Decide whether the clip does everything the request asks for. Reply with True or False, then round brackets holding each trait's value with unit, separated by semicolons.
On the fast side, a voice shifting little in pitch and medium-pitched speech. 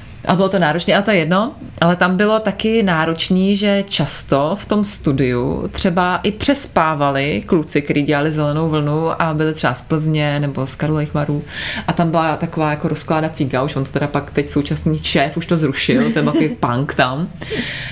False (185 wpm; 3.8 semitones; 160 Hz)